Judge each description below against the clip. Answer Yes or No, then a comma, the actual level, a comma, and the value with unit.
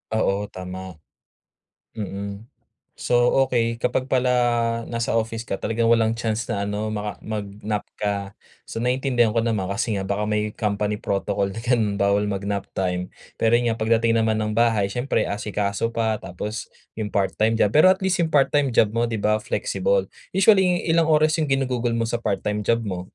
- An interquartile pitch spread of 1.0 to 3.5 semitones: Yes, narrow, 2.6 semitones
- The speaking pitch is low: Yes, low, 110 Hz